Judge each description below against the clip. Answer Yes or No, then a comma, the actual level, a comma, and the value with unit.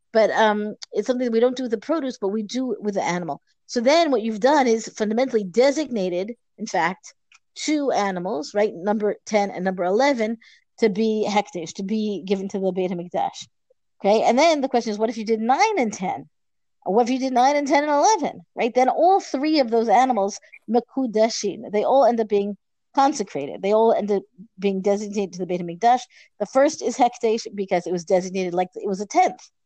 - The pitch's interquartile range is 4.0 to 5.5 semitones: Yes, average, 4.3 semitones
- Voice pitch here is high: Yes, high, 220 Hz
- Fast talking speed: Yes, fast, 210 wpm